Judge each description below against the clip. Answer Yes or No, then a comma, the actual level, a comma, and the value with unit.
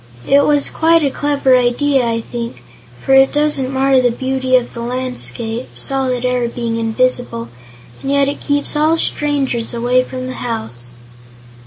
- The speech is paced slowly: No, average, 160 wpm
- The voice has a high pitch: Yes, very high, 255 Hz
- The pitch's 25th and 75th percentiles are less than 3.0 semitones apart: Yes, narrow, 2.6 semitones